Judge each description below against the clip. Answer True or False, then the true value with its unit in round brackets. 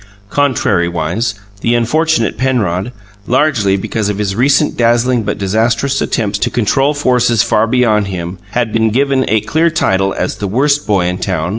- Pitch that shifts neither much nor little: True (4.6 semitones)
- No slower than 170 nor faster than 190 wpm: False (160 wpm)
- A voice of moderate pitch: False (115 Hz)